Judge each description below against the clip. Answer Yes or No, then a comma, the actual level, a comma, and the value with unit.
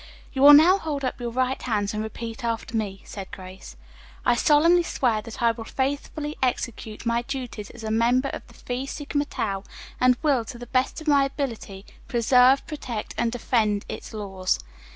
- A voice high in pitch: Yes, high, 240 Hz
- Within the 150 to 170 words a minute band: No, average, 190 wpm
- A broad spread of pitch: No, average, 3.8 semitones